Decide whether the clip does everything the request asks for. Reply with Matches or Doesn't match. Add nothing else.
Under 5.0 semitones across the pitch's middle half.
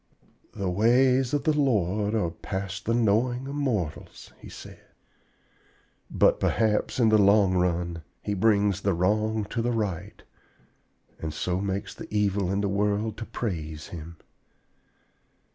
Matches